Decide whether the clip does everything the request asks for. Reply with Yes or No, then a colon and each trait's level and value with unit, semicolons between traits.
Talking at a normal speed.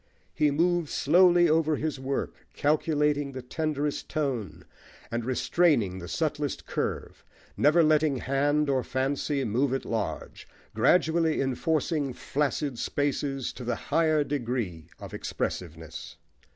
No: slow, 120 wpm